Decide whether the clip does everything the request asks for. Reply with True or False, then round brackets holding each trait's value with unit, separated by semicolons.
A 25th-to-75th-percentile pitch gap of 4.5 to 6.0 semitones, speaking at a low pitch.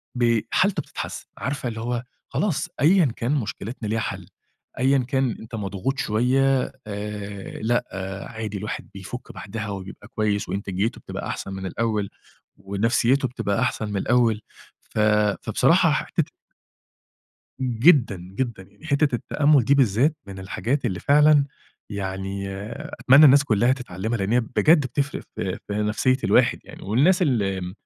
True (4.8 semitones; 115 Hz)